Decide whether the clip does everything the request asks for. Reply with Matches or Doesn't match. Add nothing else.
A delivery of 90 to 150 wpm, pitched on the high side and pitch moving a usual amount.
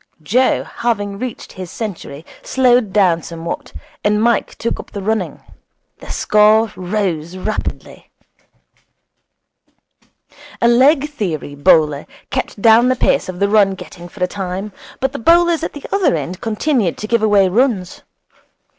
Matches